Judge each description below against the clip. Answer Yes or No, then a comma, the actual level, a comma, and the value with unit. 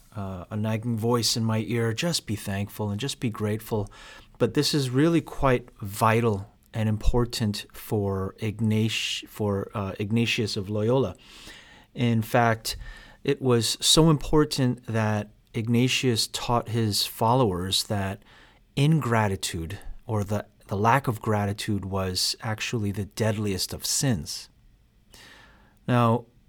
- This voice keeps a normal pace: No, slow, 125 wpm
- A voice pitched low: Yes, low, 110 Hz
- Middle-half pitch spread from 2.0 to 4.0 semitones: Yes, average, 2.7 semitones